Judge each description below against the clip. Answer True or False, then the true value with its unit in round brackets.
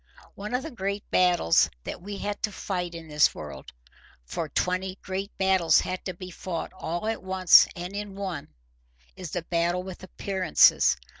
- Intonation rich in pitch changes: False (2.9 semitones)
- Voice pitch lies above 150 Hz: True (185 Hz)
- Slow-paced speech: False (160 wpm)